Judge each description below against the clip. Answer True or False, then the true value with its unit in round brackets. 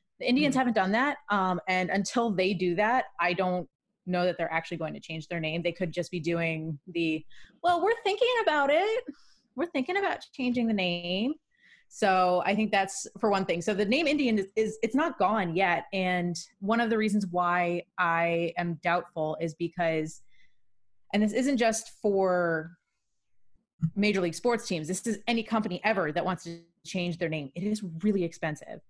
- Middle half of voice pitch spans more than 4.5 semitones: True (5.0 semitones)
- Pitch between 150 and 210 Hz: True (185 Hz)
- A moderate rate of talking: True (190 wpm)